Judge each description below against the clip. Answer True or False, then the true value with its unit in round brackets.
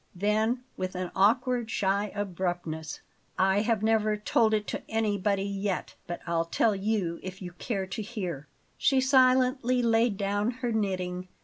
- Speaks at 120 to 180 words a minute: True (150 wpm)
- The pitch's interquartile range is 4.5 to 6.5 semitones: False (3.3 semitones)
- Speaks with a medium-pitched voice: False (205 Hz)